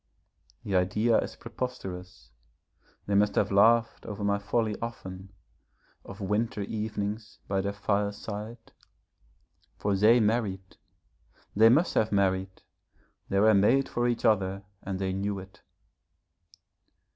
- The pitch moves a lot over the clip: No, narrow, 2.5 semitones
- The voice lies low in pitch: Yes, low, 100 Hz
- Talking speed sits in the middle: No, slow, 120 wpm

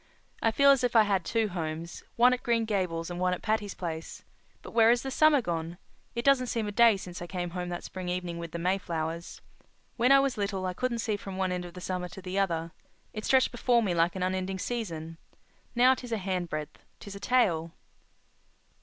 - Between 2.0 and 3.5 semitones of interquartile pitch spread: No, average, 4.9 semitones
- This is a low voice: No, high, 190 Hz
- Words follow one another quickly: Yes, fast, 215 wpm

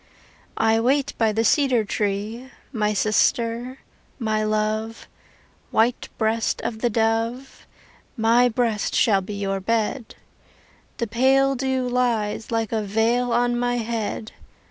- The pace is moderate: No, slow, 125 wpm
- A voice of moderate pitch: No, high, 225 Hz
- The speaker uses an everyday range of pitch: No, narrow, 2.2 semitones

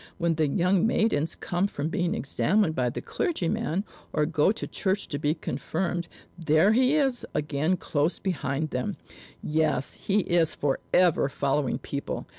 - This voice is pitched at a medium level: Yes, medium, 165 Hz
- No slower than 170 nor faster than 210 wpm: No, average, 150 wpm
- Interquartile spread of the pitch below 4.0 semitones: No, average, 4.6 semitones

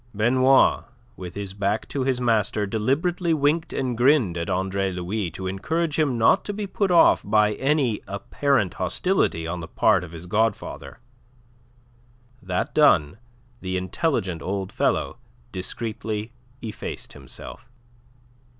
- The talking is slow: Yes, slow, 130 wpm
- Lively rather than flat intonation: Yes, wide, 6.7 semitones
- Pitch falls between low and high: No, low, 110 Hz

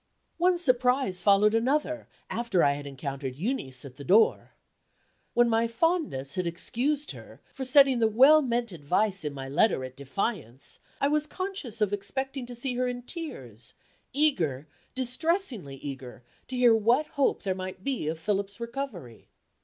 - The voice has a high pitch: Yes, high, 225 Hz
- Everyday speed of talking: Yes, average, 160 wpm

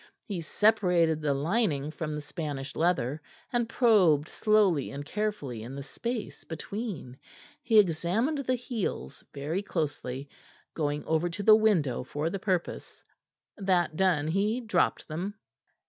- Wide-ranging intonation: Yes, wide, 6.3 semitones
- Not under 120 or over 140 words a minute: Yes, slow, 135 wpm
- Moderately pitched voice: Yes, medium, 170 Hz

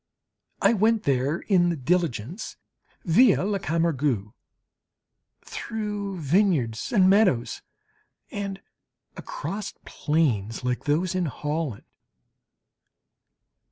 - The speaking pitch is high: No, medium, 170 Hz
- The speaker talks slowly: Yes, slow, 85 wpm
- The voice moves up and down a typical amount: No, wide, 6.4 semitones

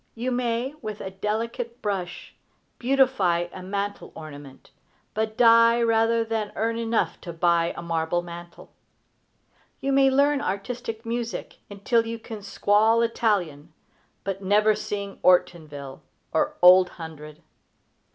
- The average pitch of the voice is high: Yes, high, 210 Hz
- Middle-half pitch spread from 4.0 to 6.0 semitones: Yes, average, 4.8 semitones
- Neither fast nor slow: No, slow, 120 wpm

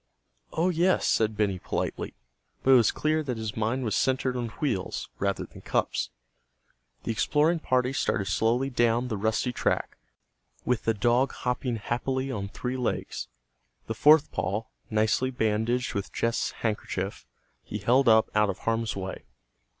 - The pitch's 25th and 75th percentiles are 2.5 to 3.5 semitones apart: Yes, average, 3.2 semitones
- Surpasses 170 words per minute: No, average, 155 wpm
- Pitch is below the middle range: Yes, low, 120 Hz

